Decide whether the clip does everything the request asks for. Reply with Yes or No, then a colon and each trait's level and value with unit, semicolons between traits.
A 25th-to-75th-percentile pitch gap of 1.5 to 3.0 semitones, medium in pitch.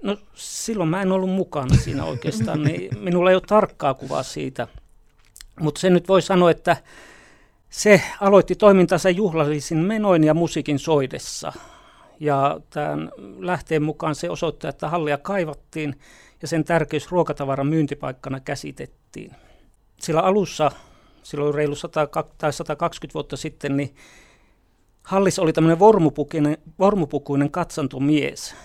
No: average, 3.7 semitones; medium, 155 Hz